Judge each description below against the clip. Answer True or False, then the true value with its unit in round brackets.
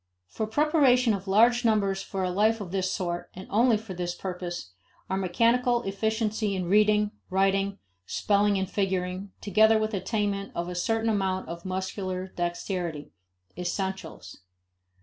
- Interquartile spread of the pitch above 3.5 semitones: False (2.8 semitones)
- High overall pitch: True (195 Hz)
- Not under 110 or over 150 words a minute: True (145 wpm)